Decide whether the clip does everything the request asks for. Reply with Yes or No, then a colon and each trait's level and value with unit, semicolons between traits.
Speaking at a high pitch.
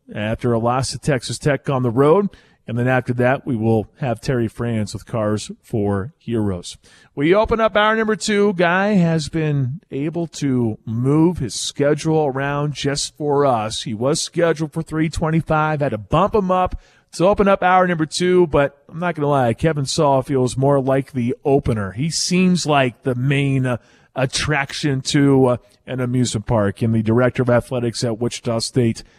No: medium, 140 Hz